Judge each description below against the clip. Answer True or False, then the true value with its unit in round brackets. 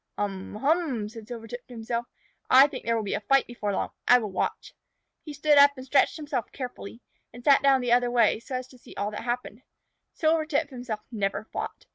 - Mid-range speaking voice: False (245 Hz)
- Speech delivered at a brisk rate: True (210 wpm)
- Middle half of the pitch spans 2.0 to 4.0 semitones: True (3.7 semitones)